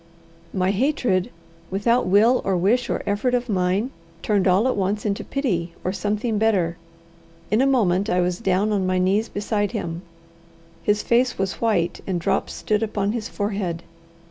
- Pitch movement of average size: Yes, average, 3.2 semitones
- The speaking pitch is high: Yes, high, 205 Hz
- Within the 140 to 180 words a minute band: Yes, average, 170 wpm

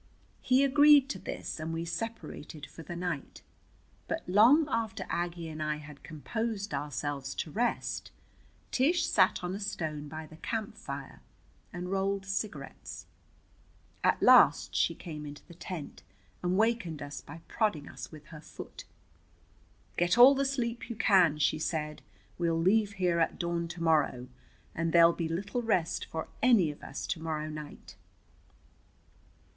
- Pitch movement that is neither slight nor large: No, wide, 5.8 semitones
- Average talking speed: Yes, average, 155 wpm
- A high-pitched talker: No, medium, 170 Hz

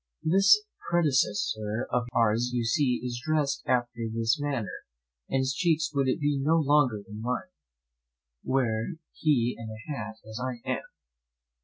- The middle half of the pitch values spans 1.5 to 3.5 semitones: No, average, 4.3 semitones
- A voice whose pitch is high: No, low, 125 Hz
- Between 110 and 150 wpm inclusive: Yes, average, 145 wpm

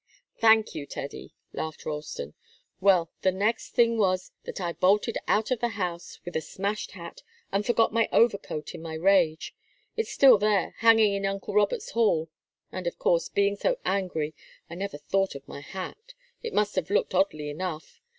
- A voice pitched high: Yes, high, 195 Hz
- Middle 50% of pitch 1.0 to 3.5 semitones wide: No, average, 4.2 semitones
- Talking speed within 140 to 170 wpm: No, average, 180 wpm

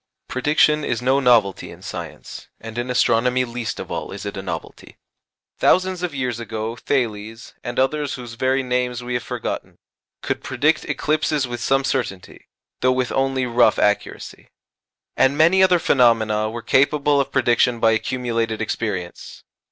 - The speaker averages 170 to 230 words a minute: No, average, 155 wpm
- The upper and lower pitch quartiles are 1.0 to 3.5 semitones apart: Yes, average, 3.0 semitones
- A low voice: Yes, low, 125 Hz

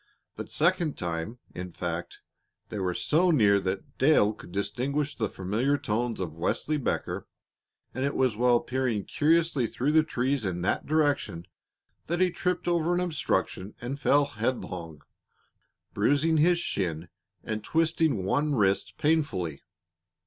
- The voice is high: No, low, 125 Hz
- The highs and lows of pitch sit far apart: Yes, wide, 7.9 semitones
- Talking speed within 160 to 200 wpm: No, average, 140 wpm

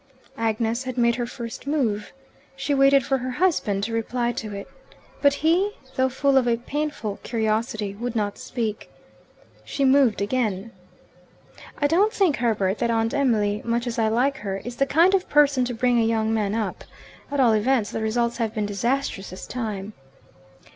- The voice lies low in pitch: No, high, 235 Hz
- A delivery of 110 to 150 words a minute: No, average, 180 wpm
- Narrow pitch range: No, average, 3.7 semitones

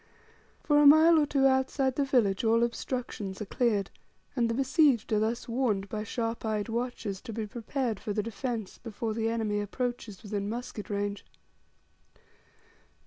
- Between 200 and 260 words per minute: No, average, 160 wpm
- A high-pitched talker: Yes, high, 230 Hz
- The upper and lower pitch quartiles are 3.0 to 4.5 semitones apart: Yes, average, 3.4 semitones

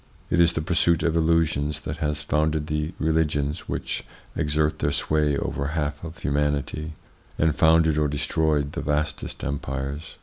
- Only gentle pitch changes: Yes, narrow, 1.5 semitones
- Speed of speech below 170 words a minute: Yes, average, 160 wpm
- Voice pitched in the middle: No, very low, 75 Hz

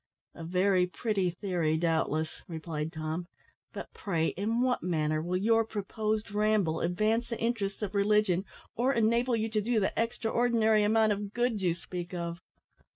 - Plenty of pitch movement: No, average, 4.3 semitones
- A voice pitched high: Yes, high, 200 Hz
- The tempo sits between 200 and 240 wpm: No, average, 160 wpm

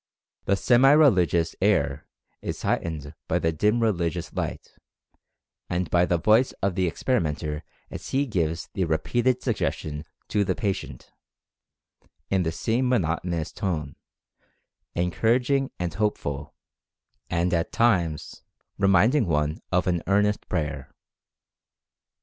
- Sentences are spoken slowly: Yes, slow, 120 wpm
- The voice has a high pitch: No, very low, 90 Hz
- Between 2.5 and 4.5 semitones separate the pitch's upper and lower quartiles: No, average, 5.0 semitones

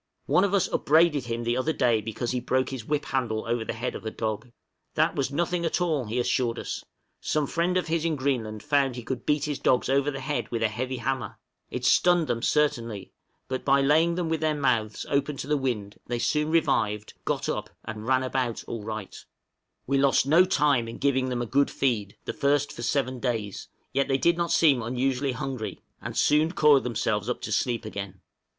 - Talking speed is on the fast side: Yes, fast, 215 wpm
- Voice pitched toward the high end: No, low, 130 Hz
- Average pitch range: Yes, average, 4.1 semitones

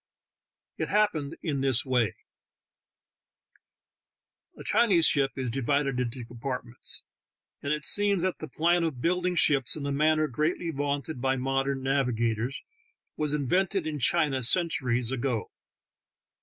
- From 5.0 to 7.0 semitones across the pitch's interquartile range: No, average, 3.9 semitones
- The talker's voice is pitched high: No, medium, 140 Hz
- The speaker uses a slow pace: Yes, slow, 130 wpm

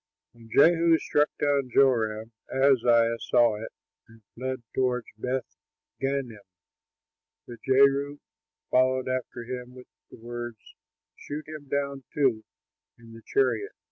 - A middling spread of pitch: Yes, average, 3.0 semitones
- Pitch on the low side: Yes, low, 130 Hz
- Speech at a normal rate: No, slow, 120 wpm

